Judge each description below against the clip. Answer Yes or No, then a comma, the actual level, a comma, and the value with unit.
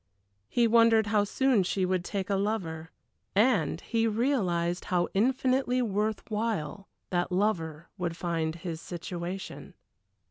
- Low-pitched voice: No, high, 195 Hz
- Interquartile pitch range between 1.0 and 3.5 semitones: No, average, 4.5 semitones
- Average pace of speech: No, slow, 130 wpm